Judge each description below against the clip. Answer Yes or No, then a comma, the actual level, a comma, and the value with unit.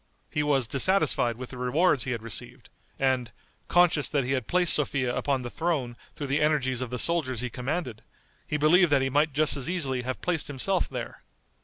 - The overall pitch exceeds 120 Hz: Yes, low, 135 Hz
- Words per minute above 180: Yes, average, 200 wpm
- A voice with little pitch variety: No, average, 3.5 semitones